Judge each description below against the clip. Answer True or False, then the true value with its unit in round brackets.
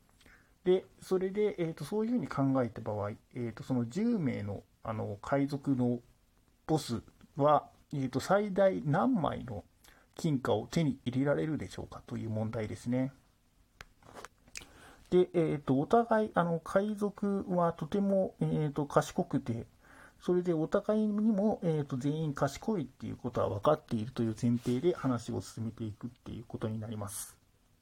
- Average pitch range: False (7.2 semitones)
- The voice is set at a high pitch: False (135 Hz)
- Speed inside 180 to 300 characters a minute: True (295 characters per minute)